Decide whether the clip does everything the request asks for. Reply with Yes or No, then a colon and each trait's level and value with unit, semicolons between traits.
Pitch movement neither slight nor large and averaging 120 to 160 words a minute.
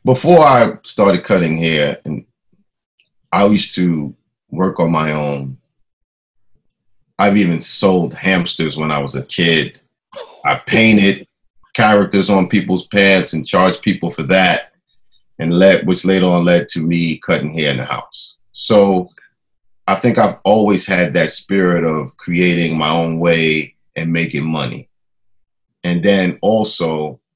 Yes: average, 3.6 semitones; average, 145 wpm